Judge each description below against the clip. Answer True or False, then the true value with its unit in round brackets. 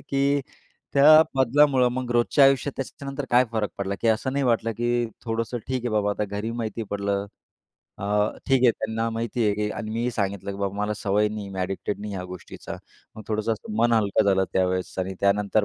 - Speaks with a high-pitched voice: False (110 Hz)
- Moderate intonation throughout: True (3.5 semitones)